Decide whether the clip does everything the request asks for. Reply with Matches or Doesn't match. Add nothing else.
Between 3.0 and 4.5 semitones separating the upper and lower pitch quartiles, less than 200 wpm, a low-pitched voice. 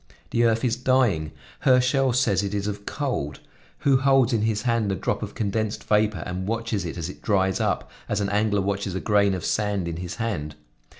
Doesn't match